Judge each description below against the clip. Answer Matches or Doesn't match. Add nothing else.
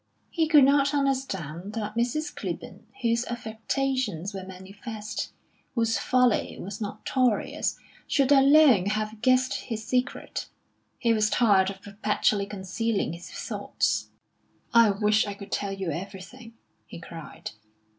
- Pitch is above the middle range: Matches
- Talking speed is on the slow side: Matches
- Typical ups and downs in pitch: Matches